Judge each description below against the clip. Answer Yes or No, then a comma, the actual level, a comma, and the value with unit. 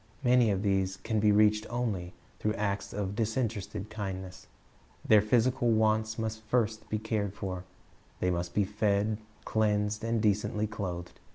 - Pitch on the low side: Yes, low, 105 Hz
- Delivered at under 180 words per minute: Yes, average, 150 wpm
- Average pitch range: No, narrow, 1.8 semitones